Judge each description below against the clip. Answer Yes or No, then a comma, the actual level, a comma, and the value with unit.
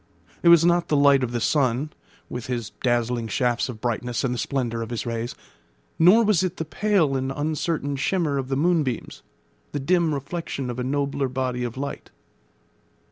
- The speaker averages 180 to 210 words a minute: Yes, average, 185 wpm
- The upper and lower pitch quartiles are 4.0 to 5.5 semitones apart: Yes, average, 4.4 semitones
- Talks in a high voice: No, low, 135 Hz